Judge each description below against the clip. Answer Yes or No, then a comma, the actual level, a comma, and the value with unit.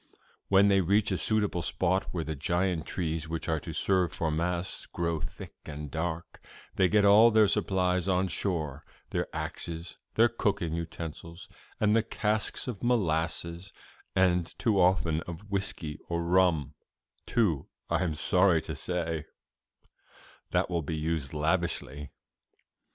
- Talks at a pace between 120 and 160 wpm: Yes, average, 145 wpm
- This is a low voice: Yes, very low, 85 Hz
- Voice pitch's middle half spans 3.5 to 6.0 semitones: No, average, 3.0 semitones